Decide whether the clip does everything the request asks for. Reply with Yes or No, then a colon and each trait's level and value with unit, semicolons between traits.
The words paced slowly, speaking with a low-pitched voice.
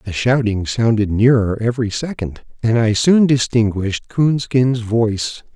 Yes: slow, 130 wpm; low, 115 Hz